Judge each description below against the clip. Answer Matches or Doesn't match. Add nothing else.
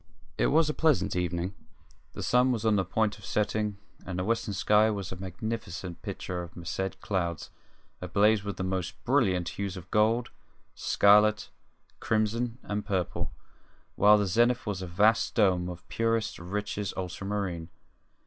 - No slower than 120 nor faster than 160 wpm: Matches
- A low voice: Matches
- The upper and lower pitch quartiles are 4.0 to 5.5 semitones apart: Doesn't match